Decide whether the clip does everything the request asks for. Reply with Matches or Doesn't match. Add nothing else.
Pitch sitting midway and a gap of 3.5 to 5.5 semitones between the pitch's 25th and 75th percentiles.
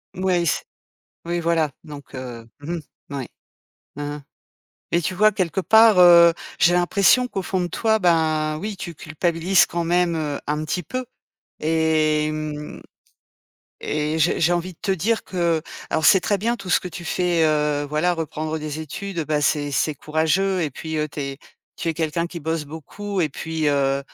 Doesn't match